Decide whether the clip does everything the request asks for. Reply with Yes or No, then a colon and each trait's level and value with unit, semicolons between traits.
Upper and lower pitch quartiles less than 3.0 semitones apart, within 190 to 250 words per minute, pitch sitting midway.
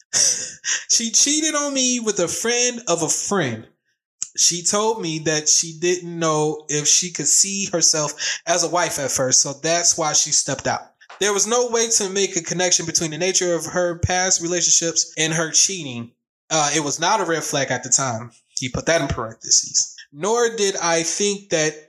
No: average, 4.2 semitones; average, 195 wpm; medium, 170 Hz